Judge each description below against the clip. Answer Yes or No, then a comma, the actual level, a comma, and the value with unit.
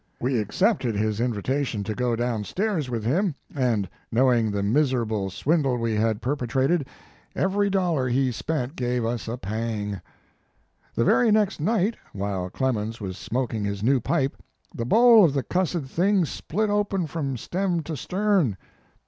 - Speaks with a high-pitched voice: No, low, 130 Hz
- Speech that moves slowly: No, average, 160 wpm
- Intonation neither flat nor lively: No, wide, 7.4 semitones